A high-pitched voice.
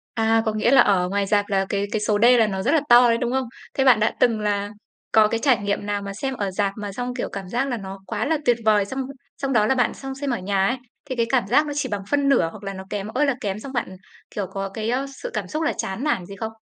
Yes: high, 220 Hz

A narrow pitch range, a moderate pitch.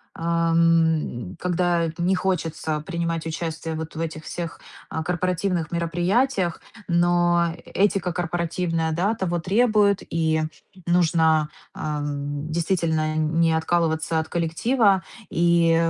Yes: narrow, 1.6 semitones; medium, 165 Hz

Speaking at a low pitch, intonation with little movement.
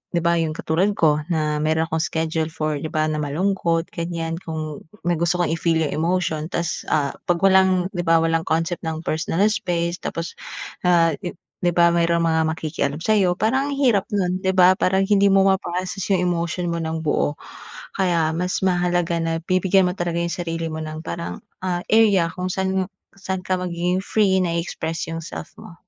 No: medium, 170 Hz; narrow, 2.3 semitones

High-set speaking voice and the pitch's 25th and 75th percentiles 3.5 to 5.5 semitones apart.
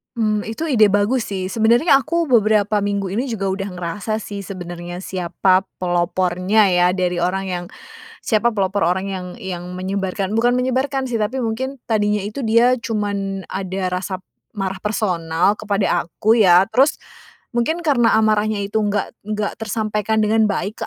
No: high, 205 Hz; average, 2.9 semitones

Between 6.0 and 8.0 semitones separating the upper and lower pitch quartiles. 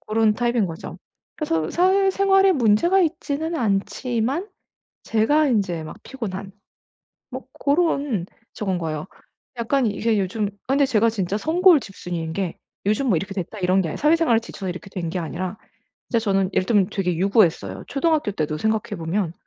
Yes: wide, 7.0 semitones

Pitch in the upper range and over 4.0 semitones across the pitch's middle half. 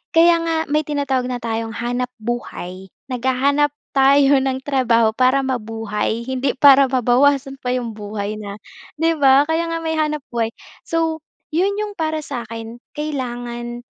No: very high, 260 Hz; average, 3.7 semitones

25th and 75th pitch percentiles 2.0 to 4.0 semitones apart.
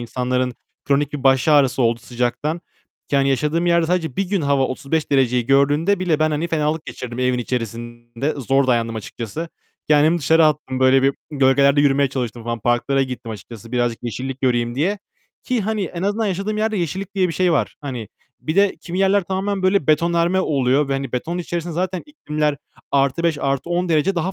No: average, 5.2 semitones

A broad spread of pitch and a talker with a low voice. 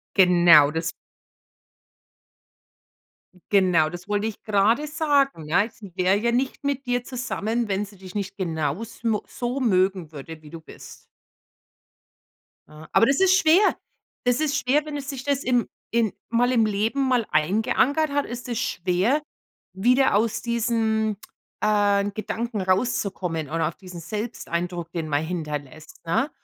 No: wide, 5.7 semitones; high, 210 Hz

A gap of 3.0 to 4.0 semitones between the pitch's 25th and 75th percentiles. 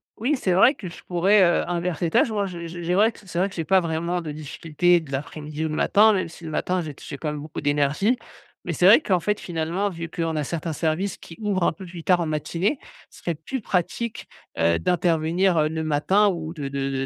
Yes: average, 3.3 semitones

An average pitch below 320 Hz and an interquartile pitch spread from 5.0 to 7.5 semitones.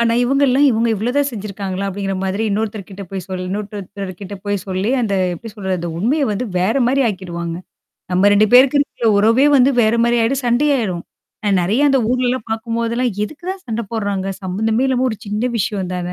No: high, 220 Hz; average, 4.1 semitones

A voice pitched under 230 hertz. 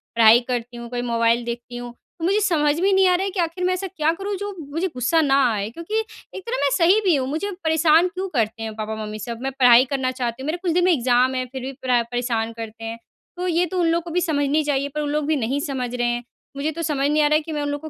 No: very high, 290 Hz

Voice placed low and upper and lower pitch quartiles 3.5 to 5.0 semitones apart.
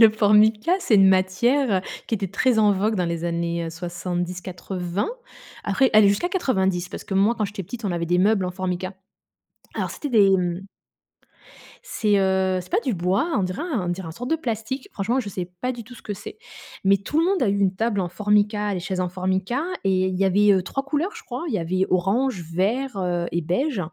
No: high, 195 Hz; average, 3.8 semitones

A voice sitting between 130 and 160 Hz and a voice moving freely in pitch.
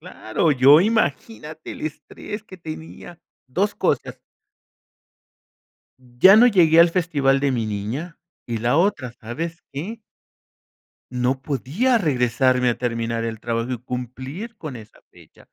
Yes: medium, 140 Hz; wide, 5.9 semitones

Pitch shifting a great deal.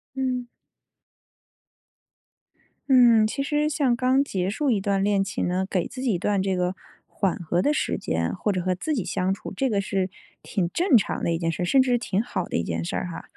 Yes: wide, 5.8 semitones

